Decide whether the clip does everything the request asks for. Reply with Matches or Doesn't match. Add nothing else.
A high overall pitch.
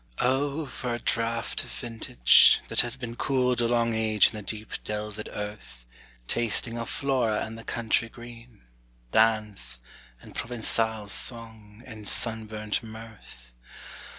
Doesn't match